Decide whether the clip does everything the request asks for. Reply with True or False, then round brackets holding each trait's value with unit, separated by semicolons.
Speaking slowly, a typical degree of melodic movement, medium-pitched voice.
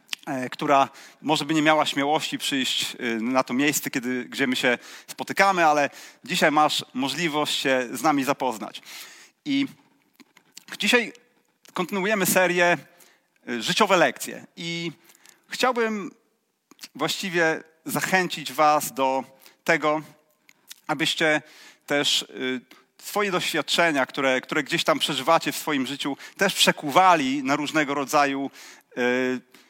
True (105 wpm; 4.0 semitones; 150 Hz)